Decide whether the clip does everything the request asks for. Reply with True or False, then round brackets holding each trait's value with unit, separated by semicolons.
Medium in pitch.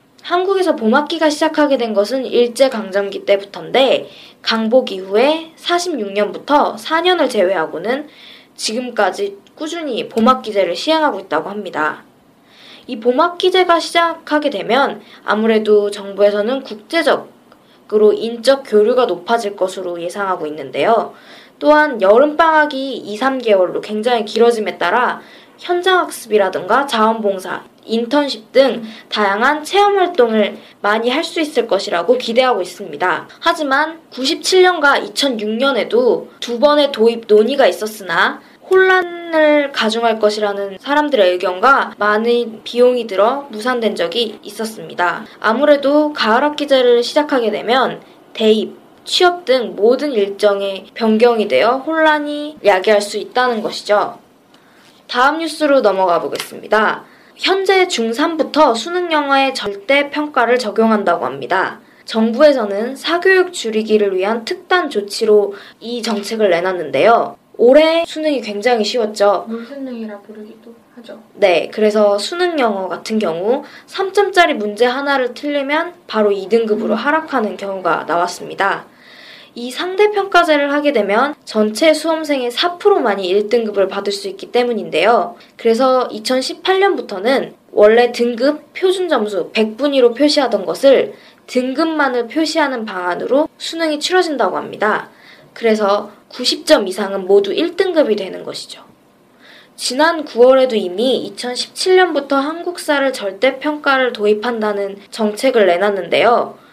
False (245 Hz)